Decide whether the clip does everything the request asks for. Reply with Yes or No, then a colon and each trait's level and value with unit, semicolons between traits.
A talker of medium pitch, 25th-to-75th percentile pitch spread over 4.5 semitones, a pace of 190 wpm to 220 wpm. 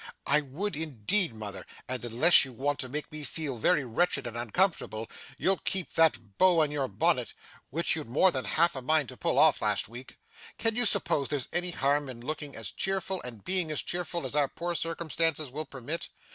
Yes: medium, 150 Hz; average, 5.1 semitones; average, 200 wpm